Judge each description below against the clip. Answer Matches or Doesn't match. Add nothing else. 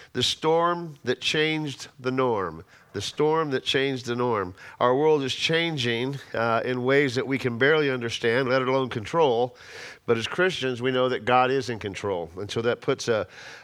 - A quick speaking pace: Doesn't match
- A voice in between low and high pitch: Doesn't match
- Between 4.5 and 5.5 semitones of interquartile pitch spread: Doesn't match